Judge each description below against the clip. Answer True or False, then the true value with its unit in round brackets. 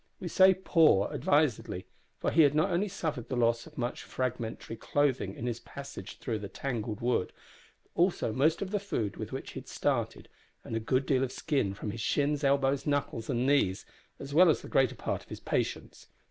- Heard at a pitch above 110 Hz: True (135 Hz)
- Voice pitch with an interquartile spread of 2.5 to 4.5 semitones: False (4.9 semitones)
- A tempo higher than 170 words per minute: True (205 wpm)